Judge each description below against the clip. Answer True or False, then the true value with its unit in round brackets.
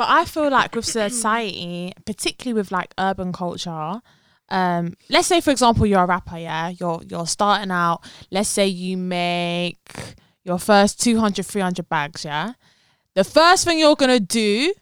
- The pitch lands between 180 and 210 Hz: True (190 Hz)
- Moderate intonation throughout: True (4.6 semitones)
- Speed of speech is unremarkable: True (165 wpm)